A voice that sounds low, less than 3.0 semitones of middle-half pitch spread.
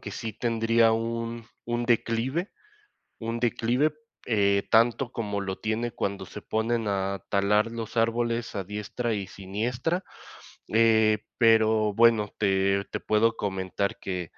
Yes: low, 110 Hz; narrow, 2.4 semitones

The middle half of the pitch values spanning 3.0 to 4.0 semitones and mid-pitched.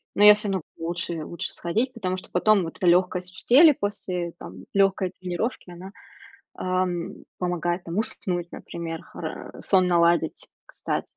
No: narrow, 2.5 semitones; medium, 180 Hz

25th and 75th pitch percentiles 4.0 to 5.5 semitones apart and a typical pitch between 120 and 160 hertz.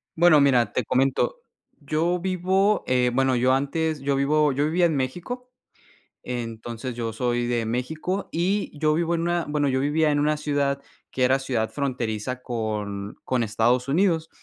Yes: average, 4.6 semitones; medium, 140 Hz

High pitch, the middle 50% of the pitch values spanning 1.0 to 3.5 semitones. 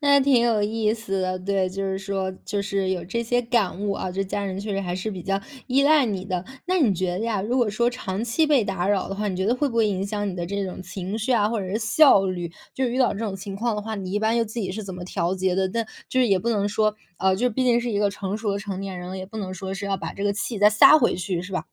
Yes: high, 200 Hz; average, 3.2 semitones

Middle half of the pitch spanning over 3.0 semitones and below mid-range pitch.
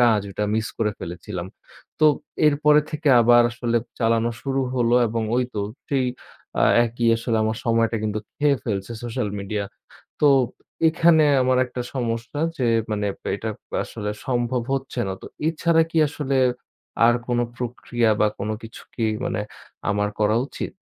Yes: average, 3.4 semitones; low, 120 Hz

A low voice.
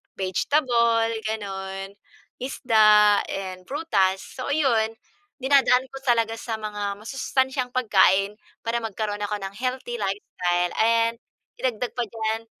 No: high, 220 Hz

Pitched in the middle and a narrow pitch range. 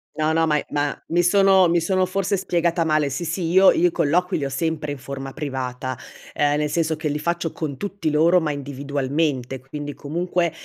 No: medium, 155 Hz; average, 3.3 semitones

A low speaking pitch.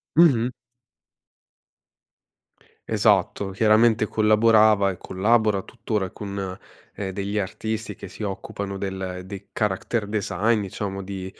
Yes: low, 105 Hz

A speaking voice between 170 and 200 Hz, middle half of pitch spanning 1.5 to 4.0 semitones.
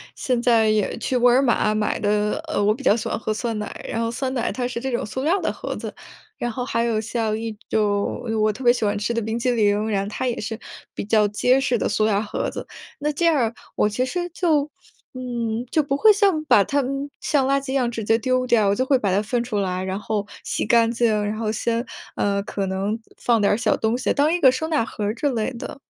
No: high, 230 Hz; average, 3.4 semitones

